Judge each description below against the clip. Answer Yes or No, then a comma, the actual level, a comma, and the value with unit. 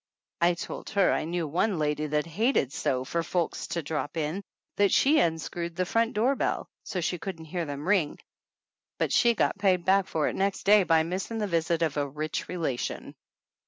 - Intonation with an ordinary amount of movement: Yes, average, 3.9 semitones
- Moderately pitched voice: Yes, medium, 170 Hz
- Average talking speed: Yes, average, 195 wpm